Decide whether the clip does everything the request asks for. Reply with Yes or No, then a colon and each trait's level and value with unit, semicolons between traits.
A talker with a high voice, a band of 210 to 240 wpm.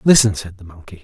No: low, 100 Hz; fast, 230 wpm